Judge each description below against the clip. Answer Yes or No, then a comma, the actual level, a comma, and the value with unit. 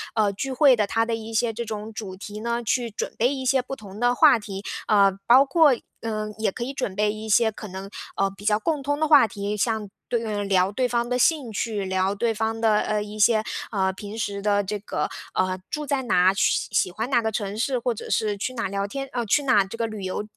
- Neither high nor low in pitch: No, high, 220 Hz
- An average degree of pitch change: Yes, average, 3.0 semitones